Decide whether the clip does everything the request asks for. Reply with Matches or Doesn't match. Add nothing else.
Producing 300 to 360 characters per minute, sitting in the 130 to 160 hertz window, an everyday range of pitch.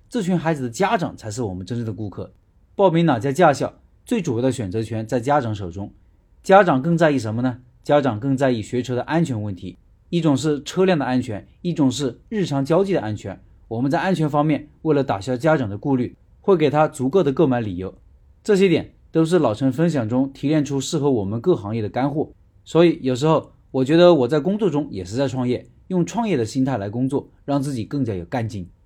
Doesn't match